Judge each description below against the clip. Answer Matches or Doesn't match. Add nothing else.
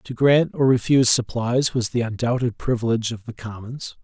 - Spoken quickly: Doesn't match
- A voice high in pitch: Doesn't match